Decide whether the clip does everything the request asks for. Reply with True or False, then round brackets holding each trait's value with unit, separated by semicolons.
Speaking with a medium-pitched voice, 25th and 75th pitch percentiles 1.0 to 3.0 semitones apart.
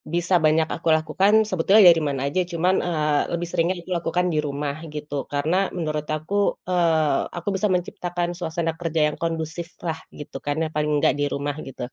True (165 Hz; 2.7 semitones)